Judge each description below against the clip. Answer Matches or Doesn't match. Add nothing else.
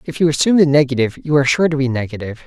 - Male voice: Matches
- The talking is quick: Matches